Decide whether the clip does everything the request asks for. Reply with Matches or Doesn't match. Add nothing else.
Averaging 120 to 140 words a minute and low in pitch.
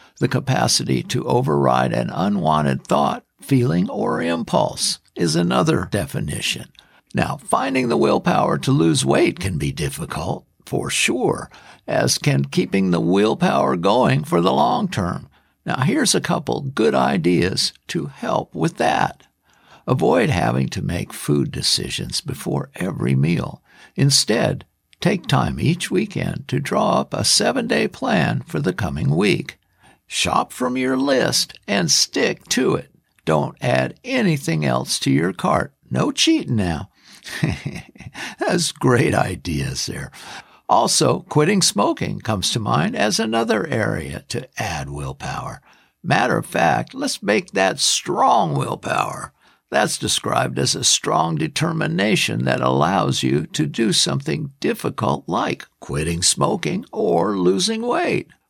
Matches